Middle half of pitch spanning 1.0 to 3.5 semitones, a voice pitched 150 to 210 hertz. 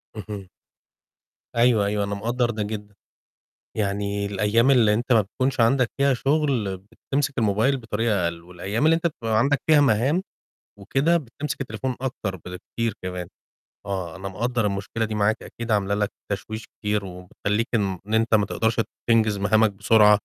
No: average, 3.2 semitones; low, 110 Hz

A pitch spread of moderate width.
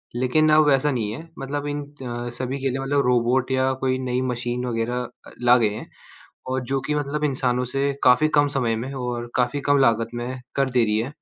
No: narrow, 2.3 semitones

